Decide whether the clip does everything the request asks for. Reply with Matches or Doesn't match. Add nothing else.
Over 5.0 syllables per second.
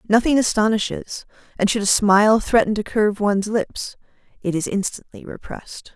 Matches